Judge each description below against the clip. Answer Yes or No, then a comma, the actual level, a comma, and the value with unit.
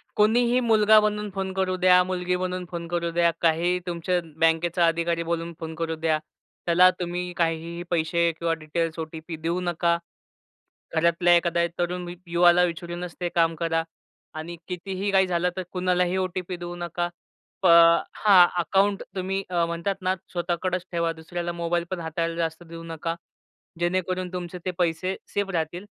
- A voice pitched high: No, medium, 175 Hz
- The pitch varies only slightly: Yes, narrow, 1.5 semitones